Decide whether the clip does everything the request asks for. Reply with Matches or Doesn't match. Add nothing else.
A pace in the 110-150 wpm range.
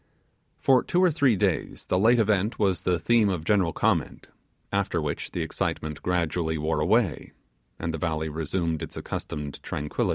Doesn't match